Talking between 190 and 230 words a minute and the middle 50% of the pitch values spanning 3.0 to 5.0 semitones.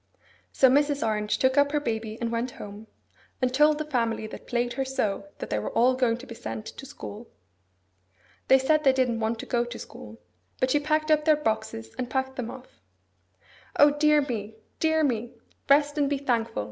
Yes: average, 200 wpm; average, 4.1 semitones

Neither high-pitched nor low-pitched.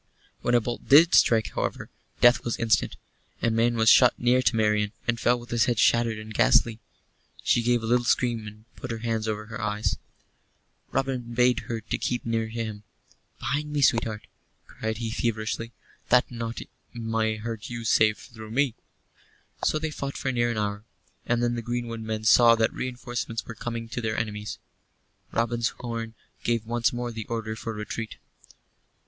No: low, 115 Hz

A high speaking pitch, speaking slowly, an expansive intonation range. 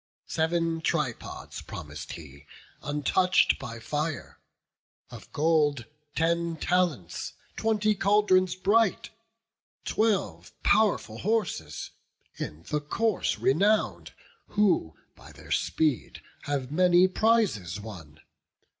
No: medium, 165 Hz; slow, 95 wpm; wide, 8.0 semitones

